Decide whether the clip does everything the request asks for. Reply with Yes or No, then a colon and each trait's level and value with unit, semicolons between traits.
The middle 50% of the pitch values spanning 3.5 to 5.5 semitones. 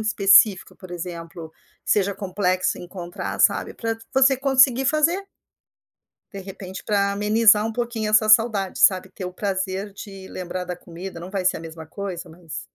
No: average, 3.1 semitones